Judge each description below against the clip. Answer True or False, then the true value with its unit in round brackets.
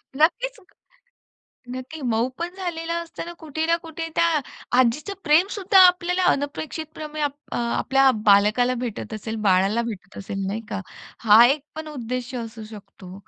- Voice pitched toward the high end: True (270 Hz)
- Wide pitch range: True (6.5 semitones)